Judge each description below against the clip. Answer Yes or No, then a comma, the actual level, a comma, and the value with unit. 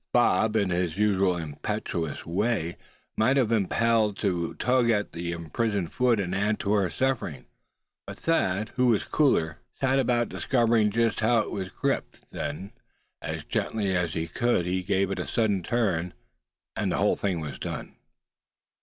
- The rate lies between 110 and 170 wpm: Yes, average, 165 wpm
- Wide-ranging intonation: No, average, 4.6 semitones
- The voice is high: No, low, 100 Hz